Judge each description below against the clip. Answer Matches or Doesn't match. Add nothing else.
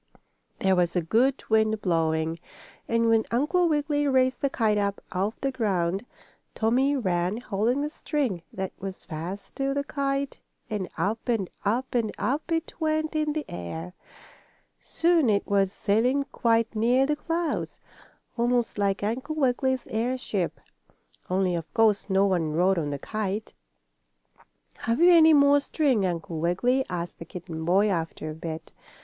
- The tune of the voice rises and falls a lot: Matches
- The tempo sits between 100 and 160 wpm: Matches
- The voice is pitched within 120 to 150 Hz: Doesn't match